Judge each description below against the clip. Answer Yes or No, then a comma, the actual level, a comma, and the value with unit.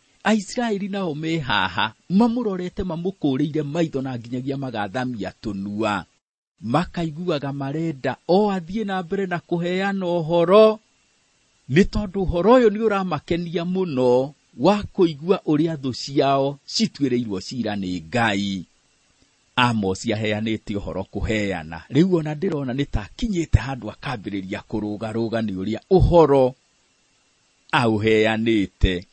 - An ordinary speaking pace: No, slow, 105 wpm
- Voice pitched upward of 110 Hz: Yes, medium, 140 Hz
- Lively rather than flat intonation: Yes, wide, 8.5 semitones